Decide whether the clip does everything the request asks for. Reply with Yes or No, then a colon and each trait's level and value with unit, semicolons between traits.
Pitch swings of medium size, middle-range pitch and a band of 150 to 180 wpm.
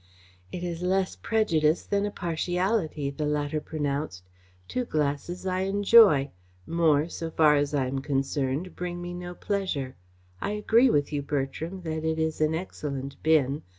Yes: average, 3.9 semitones; medium, 160 Hz; average, 155 wpm